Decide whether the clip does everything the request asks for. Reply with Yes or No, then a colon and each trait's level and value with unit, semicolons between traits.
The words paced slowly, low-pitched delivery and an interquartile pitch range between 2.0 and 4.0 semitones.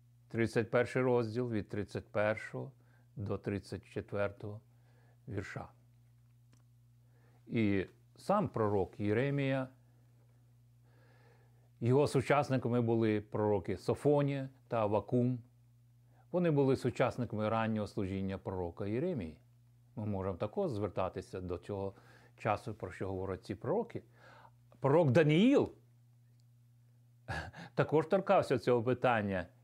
Yes: slow, 85 wpm; low, 120 Hz; average, 2.9 semitones